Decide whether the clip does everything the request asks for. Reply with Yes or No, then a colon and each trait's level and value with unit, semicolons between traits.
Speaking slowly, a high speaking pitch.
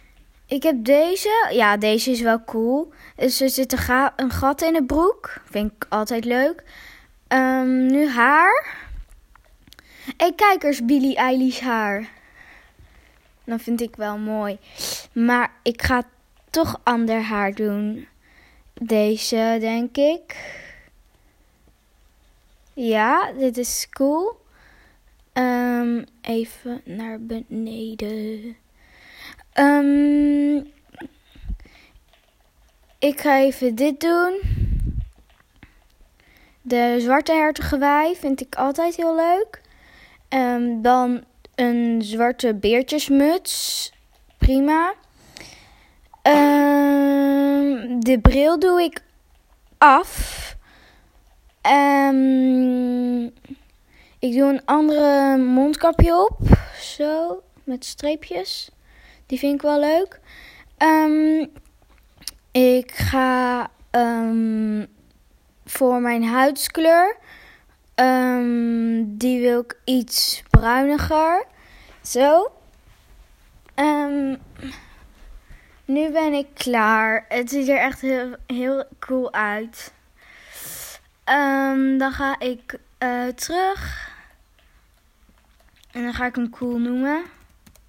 Yes: slow, 90 wpm; very high, 260 Hz